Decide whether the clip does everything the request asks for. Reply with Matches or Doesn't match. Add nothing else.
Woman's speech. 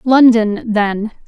Matches